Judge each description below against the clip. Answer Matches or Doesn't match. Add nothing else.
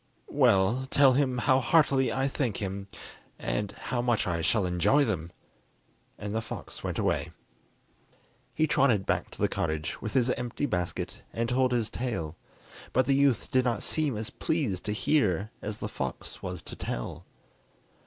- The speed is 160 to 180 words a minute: Matches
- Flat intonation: Doesn't match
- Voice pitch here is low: Matches